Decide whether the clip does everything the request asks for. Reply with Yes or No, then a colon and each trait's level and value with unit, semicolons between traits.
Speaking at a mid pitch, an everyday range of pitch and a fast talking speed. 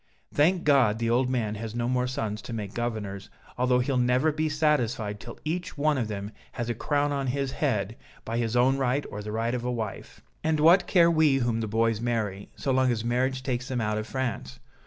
No: low, 125 Hz; average, 3.6 semitones; fast, 220 wpm